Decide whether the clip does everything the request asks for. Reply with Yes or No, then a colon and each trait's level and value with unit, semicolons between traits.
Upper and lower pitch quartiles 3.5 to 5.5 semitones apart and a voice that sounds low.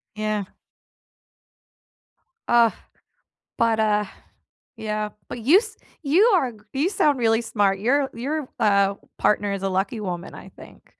No: average, 4.5 semitones; high, 220 Hz